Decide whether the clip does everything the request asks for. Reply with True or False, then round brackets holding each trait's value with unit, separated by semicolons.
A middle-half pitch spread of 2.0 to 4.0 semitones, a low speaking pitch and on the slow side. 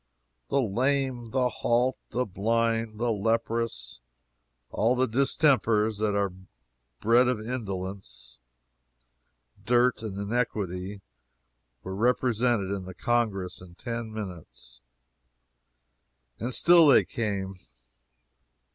True (3.7 semitones; 115 Hz; 100 wpm)